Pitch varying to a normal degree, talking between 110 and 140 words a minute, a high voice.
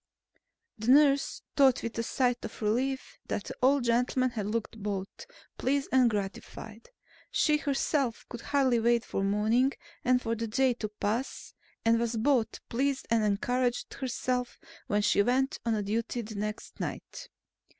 No: average, 3.2 semitones; average, 155 wpm; high, 235 Hz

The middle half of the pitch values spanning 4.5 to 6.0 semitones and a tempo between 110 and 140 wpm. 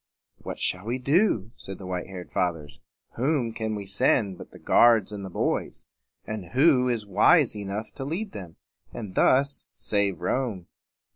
No: average, 5.1 semitones; average, 165 wpm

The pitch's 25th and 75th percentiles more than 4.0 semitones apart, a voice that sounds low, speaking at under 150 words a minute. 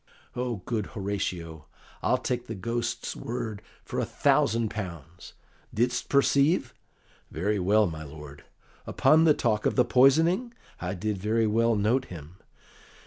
Yes: average, 5.2 semitones; low, 110 Hz; average, 140 wpm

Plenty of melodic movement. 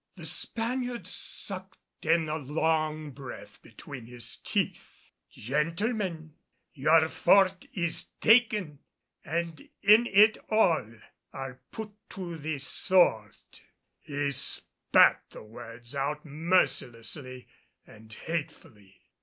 Yes: wide, 6.0 semitones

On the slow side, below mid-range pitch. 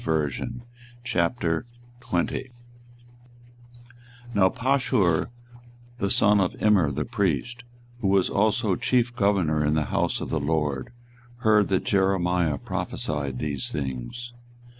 Yes: slow, 105 wpm; very low, 95 Hz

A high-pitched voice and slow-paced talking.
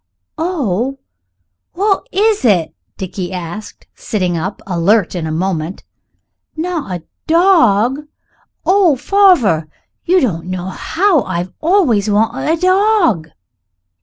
Yes: high, 225 Hz; slow, 110 wpm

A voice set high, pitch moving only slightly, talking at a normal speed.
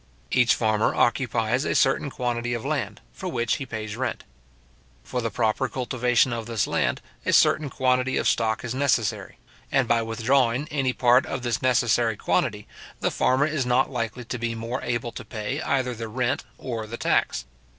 No: low, 120 Hz; narrow, 2.2 semitones; average, 180 wpm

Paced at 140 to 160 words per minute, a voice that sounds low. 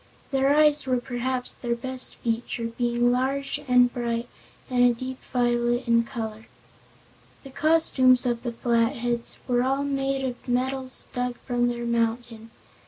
No: average, 145 wpm; high, 245 Hz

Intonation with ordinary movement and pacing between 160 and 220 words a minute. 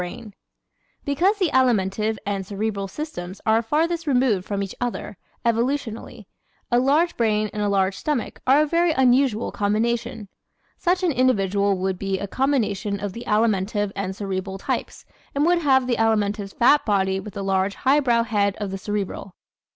Yes: average, 4.9 semitones; average, 165 wpm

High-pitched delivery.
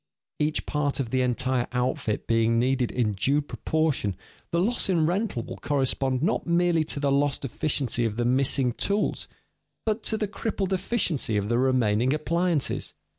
No: medium, 140 Hz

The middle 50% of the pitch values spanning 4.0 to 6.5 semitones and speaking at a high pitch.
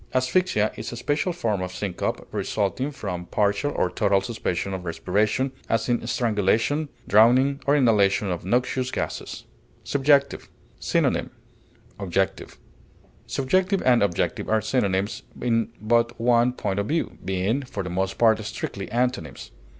No: average, 4.7 semitones; low, 110 Hz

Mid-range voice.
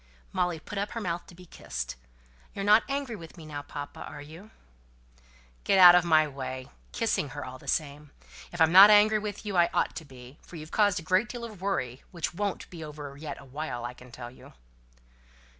Yes: medium, 165 Hz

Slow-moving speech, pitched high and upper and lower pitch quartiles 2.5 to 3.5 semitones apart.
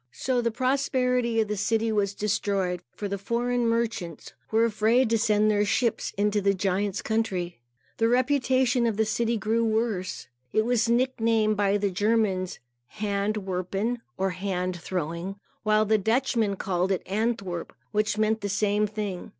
No: average, 160 wpm; high, 215 Hz; average, 2.8 semitones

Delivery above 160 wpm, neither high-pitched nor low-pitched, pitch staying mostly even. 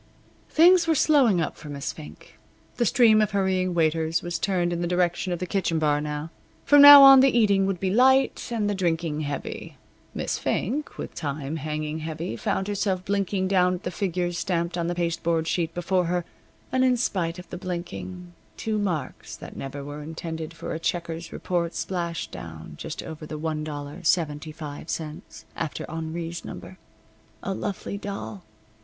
No: average, 170 wpm; medium, 170 Hz; average, 3.7 semitones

